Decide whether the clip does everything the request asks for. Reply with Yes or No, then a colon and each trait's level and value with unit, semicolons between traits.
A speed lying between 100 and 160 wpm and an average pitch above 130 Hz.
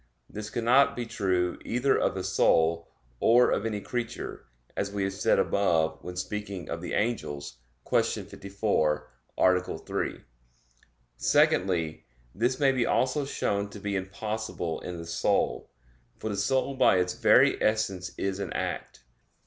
No: average, 150 wpm; low, 100 Hz